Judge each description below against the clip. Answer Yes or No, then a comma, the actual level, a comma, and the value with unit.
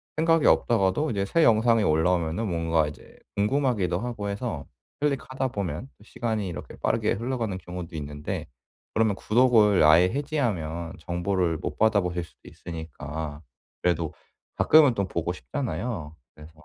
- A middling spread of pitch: No, wide, 6.0 semitones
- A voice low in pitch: Yes, low, 100 Hz